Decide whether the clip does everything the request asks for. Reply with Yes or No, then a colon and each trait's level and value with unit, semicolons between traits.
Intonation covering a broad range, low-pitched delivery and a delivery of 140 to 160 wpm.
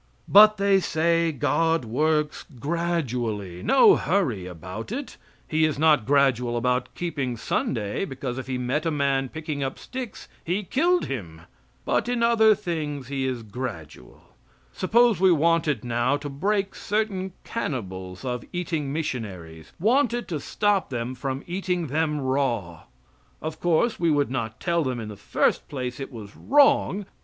No: wide, 6.3 semitones; medium, 145 Hz; average, 150 wpm